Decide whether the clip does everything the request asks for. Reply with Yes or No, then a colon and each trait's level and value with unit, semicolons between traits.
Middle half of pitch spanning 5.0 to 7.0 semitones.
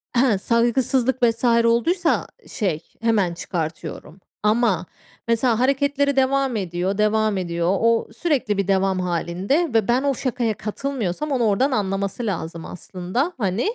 Yes: wide, 5.5 semitones